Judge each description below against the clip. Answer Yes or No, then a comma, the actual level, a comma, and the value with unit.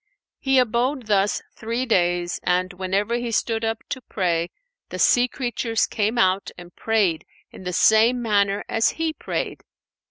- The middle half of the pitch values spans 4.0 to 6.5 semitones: Yes, average, 4.4 semitones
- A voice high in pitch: Yes, high, 220 Hz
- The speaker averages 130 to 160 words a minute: Yes, average, 155 wpm